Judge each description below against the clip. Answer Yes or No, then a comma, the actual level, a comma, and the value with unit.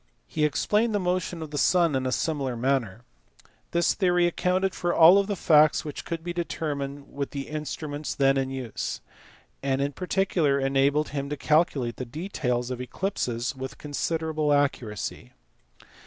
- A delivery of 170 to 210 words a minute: No, average, 155 wpm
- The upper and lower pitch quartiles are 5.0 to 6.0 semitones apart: No, average, 4.1 semitones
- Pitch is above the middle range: No, medium, 145 Hz